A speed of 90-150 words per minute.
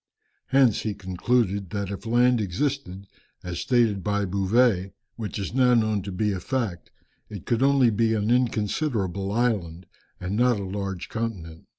No: average, 160 wpm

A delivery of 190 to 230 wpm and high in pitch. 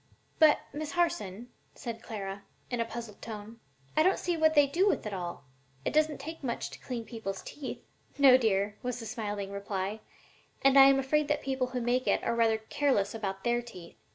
Yes: fast, 205 wpm; high, 240 Hz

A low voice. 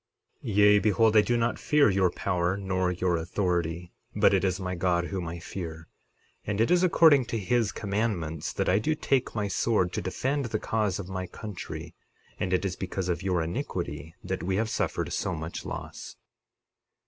Yes: very low, 95 Hz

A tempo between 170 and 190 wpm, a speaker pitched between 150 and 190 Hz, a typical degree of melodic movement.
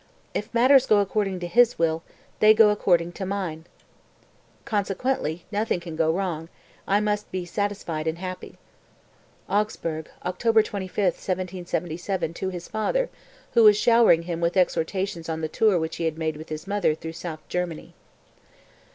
No: average, 150 wpm; medium, 185 Hz; average, 4.0 semitones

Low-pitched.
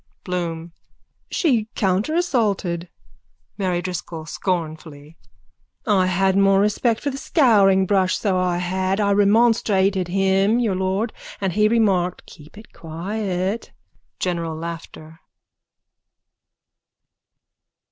No: high, 190 Hz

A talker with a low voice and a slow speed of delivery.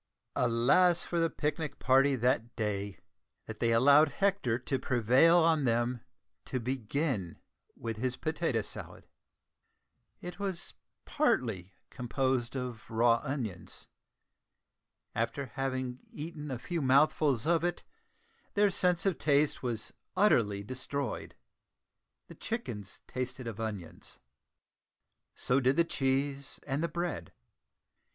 Yes: low, 130 Hz; slow, 115 wpm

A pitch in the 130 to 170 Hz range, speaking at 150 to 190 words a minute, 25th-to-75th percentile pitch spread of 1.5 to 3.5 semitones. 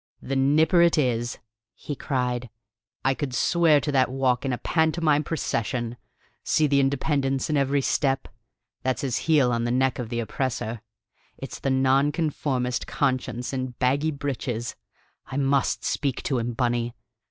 Yes: low, 135 Hz; average, 155 wpm; narrow, 2.6 semitones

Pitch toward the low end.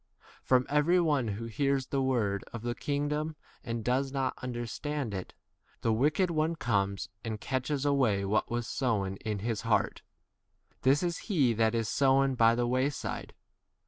Yes: low, 125 Hz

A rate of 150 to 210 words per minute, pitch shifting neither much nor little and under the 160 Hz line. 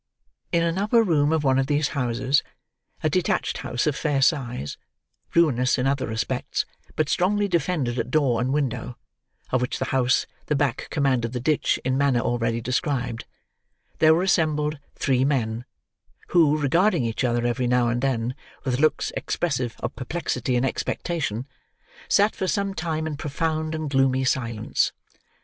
Yes: average, 155 wpm; average, 4.1 semitones; low, 135 Hz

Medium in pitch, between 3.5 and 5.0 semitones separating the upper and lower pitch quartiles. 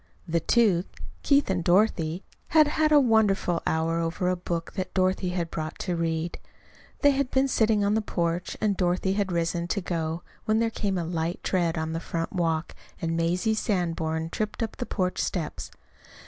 Yes: medium, 180 Hz; average, 4.2 semitones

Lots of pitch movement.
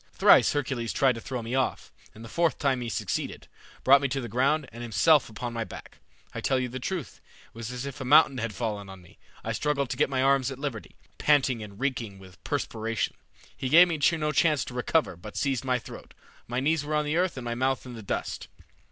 No: average, 3.7 semitones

